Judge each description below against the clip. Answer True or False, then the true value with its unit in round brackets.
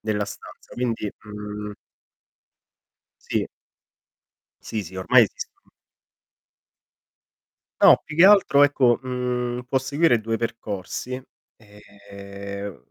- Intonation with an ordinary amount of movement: True (3.7 semitones)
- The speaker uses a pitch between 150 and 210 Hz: False (115 Hz)